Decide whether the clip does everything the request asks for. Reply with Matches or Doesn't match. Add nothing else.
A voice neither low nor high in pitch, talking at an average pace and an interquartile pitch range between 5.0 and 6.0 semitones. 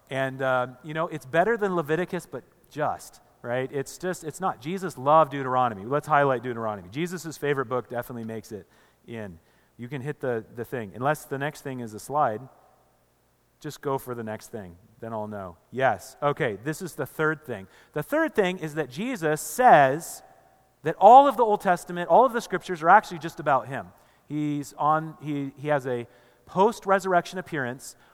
Matches